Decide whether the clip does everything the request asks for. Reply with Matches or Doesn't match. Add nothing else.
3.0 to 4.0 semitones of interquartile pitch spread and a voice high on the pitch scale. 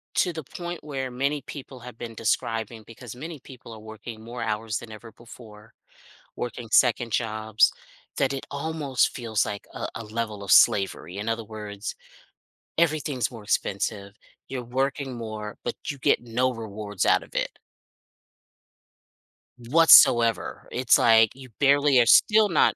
Doesn't match